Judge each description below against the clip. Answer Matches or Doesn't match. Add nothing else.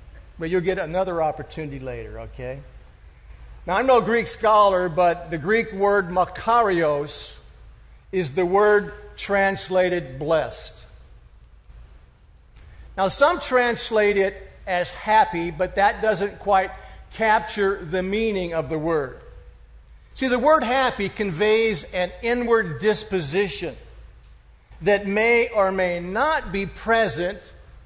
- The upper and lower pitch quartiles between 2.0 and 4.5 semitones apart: Doesn't match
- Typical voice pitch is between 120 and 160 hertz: Doesn't match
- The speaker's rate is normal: Doesn't match